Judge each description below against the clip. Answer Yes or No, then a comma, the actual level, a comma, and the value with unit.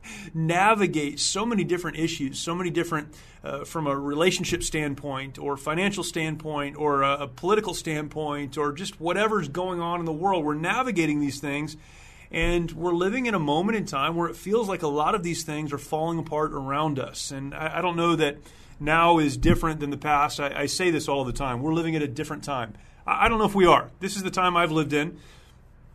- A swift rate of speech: Yes, fast, 215 wpm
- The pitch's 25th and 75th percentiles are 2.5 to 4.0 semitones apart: Yes, average, 3.3 semitones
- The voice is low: No, medium, 155 Hz